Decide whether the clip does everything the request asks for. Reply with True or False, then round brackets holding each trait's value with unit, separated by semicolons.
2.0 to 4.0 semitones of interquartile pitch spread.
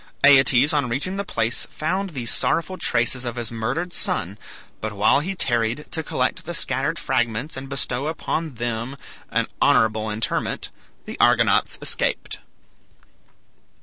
False (5.1 semitones)